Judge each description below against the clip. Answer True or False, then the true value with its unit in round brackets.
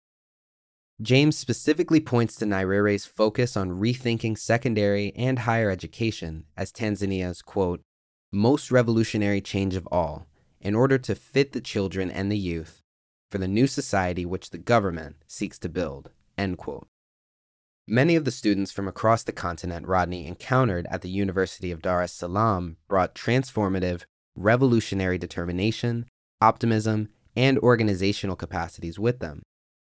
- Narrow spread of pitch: False (4.5 semitones)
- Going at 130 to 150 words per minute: True (135 wpm)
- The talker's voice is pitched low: True (100 Hz)